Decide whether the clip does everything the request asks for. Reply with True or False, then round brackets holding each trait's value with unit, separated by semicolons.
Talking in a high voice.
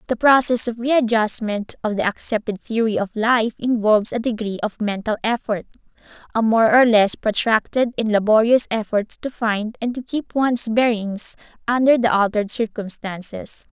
True (225 Hz)